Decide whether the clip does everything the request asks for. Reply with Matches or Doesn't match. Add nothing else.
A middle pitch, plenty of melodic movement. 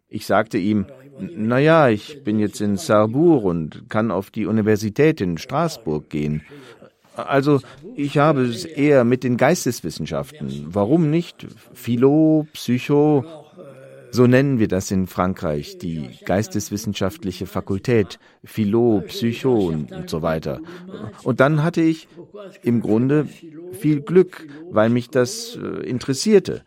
Doesn't match